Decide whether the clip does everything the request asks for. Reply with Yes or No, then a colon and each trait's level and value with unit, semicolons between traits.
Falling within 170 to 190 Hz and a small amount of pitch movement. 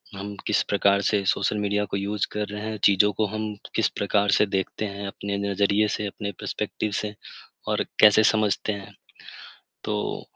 No: low, 105 Hz; narrow, 1.0 semitones